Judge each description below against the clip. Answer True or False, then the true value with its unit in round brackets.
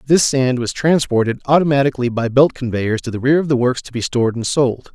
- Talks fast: True (230 wpm)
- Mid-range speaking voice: False (130 Hz)